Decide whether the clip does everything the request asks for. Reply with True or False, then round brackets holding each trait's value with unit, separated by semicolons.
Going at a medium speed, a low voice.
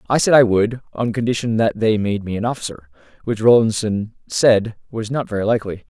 True (190 wpm; 110 Hz)